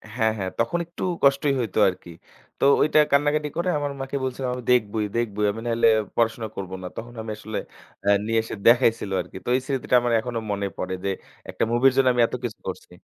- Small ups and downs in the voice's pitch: No, average, 3.6 semitones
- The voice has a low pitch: Yes, low, 120 Hz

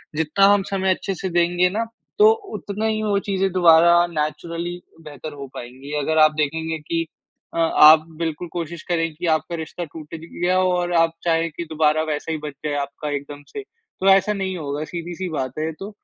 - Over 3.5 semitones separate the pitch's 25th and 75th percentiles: No, average, 3.1 semitones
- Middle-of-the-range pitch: Yes, medium, 165 Hz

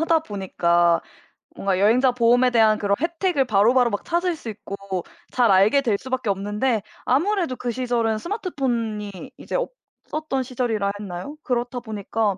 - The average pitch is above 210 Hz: Yes, high, 235 Hz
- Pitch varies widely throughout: No, average, 4.3 semitones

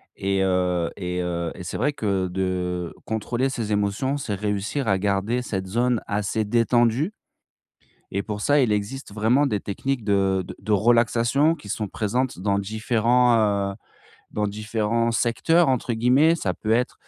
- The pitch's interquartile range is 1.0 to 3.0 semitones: No, average, 3.7 semitones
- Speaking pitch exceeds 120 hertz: No, low, 110 Hz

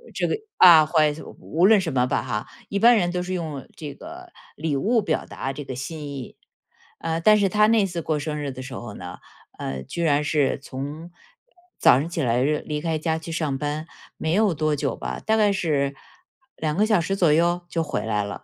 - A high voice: No, medium, 155 Hz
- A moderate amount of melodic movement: Yes, average, 4.0 semitones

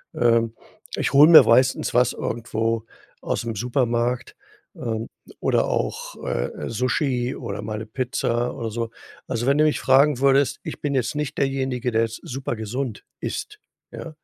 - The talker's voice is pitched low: Yes, low, 120 Hz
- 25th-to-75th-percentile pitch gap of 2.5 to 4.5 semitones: Yes, average, 2.8 semitones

